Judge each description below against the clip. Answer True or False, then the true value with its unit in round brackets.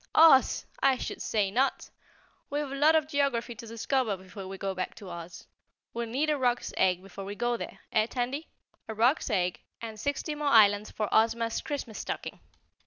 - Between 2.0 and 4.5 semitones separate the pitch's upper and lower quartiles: False (5.2 semitones)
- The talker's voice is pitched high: True (230 Hz)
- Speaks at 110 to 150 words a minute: False (185 wpm)